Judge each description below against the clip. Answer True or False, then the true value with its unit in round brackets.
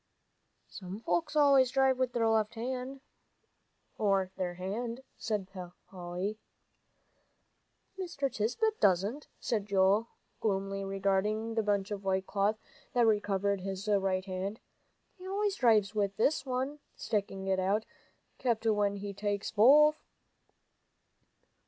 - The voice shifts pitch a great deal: False (4.3 semitones)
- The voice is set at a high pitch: True (210 Hz)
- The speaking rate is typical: False (115 wpm)